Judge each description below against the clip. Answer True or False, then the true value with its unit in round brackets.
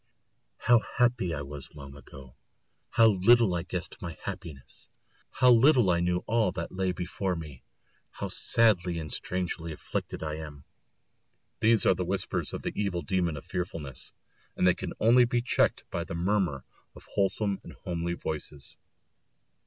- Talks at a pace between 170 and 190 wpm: False (160 wpm)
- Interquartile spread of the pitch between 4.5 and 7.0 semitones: True (4.9 semitones)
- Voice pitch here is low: True (90 Hz)